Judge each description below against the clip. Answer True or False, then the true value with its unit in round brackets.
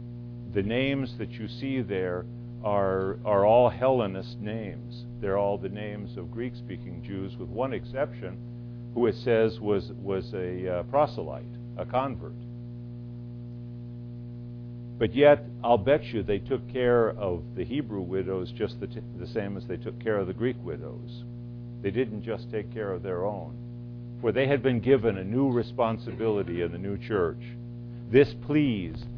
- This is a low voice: True (120 Hz)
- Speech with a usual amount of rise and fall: False (1.8 semitones)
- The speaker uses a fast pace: False (160 wpm)